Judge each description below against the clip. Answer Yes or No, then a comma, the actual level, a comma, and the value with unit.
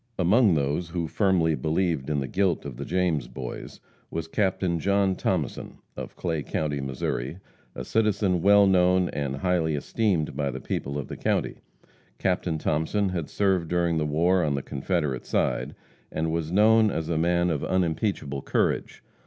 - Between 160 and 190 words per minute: Yes, average, 165 wpm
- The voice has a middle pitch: No, very low, 85 Hz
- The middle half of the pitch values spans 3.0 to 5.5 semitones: Yes, average, 3.9 semitones